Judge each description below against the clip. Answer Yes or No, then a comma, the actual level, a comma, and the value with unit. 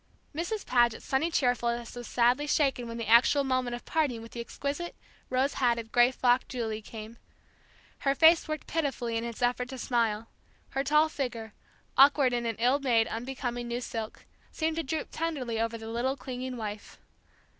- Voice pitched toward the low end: No, high, 245 Hz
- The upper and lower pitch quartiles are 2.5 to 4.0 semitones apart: Yes, average, 3.0 semitones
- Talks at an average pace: Yes, average, 175 wpm